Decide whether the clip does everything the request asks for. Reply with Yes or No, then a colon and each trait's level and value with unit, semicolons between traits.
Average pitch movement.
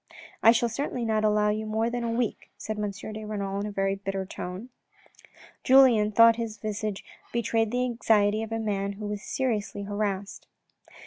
No: narrow, 2.1 semitones